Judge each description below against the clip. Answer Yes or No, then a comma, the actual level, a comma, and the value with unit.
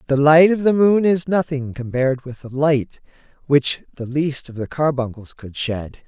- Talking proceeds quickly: No, average, 190 wpm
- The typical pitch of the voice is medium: Yes, medium, 145 Hz